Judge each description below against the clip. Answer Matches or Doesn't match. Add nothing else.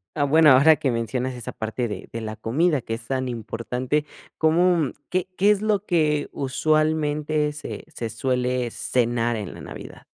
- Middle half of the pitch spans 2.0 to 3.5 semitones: Doesn't match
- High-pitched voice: Doesn't match